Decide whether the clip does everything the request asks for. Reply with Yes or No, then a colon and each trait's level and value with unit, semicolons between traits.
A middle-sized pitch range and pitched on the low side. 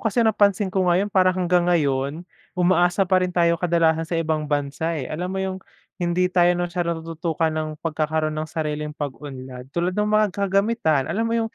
No: average, 3.1 semitones; medium, 170 Hz